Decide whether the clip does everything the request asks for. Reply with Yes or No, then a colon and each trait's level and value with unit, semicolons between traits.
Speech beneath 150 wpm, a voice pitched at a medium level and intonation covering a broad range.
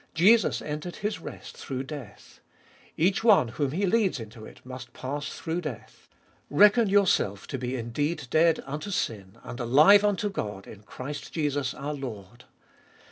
No: average, 160 wpm; medium, 145 Hz; wide, 6.6 semitones